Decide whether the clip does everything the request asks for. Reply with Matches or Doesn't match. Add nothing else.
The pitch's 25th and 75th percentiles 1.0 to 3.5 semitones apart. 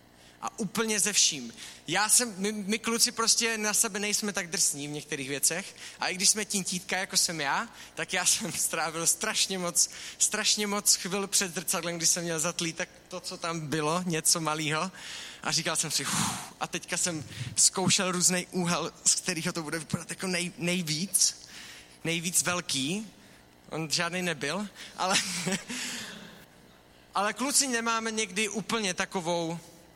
Doesn't match